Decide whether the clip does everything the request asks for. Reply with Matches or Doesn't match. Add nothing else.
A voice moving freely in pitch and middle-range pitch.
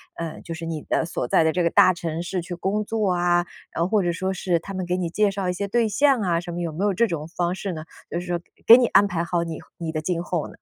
Doesn't match